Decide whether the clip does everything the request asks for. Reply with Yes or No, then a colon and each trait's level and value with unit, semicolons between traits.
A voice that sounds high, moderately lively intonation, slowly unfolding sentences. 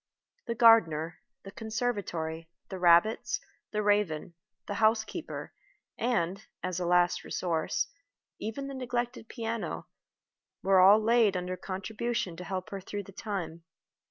Yes: high, 200 Hz; average, 4.1 semitones; slow, 130 wpm